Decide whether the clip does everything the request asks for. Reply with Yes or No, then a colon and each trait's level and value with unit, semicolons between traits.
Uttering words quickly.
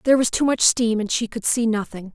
Yes: fast, 280 wpm